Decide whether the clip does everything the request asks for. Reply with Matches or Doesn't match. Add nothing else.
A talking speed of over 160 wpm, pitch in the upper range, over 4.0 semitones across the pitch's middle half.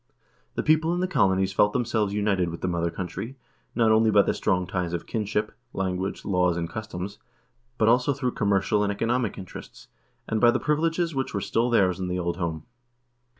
Doesn't match